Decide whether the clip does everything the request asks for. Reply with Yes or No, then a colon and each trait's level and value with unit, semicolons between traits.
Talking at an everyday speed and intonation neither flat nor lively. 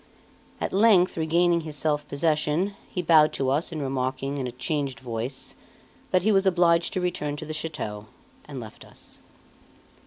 Yes: average, 160 wpm; average, 4.1 semitones